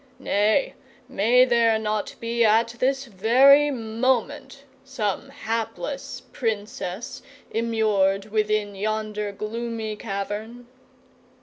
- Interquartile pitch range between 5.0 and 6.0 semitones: No, narrow, 2.6 semitones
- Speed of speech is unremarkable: No, slow, 90 wpm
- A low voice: No, high, 225 Hz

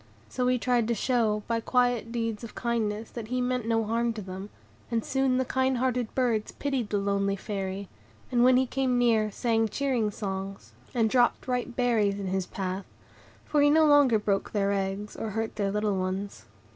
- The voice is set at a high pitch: Yes, high, 225 Hz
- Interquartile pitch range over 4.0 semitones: No, average, 3.6 semitones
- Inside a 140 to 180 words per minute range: No, average, 195 wpm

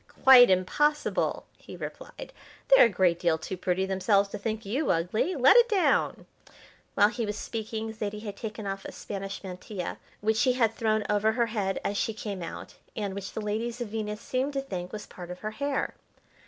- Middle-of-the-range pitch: No, high, 215 Hz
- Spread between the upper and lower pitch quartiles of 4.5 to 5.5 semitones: No, average, 3.2 semitones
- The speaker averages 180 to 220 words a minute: Yes, average, 195 wpm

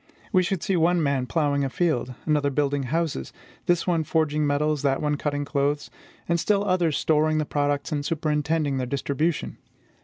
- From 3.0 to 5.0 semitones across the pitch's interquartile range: No, narrow, 2.5 semitones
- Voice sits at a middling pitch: Yes, medium, 150 Hz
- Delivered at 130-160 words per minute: No, average, 175 wpm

